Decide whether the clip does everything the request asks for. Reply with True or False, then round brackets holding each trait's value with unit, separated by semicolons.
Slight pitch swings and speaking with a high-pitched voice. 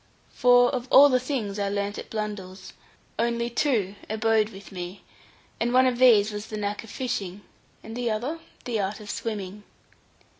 False (3.2 semitones; 220 Hz)